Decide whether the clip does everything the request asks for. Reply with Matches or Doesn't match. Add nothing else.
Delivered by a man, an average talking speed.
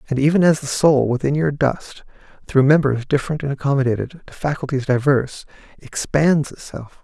Matches